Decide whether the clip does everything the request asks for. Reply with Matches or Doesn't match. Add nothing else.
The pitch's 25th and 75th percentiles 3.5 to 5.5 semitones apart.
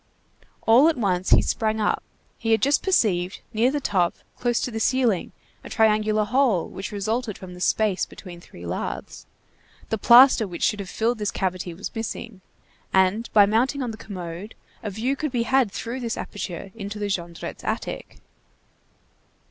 Matches